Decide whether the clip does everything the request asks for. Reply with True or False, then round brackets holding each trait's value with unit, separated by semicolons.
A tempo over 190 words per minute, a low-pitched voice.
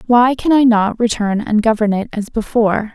False (205 wpm; 225 Hz)